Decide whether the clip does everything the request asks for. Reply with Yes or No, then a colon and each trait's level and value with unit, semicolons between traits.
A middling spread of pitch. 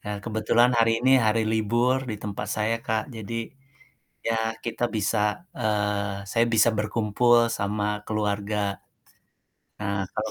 No: narrow, 1.9 semitones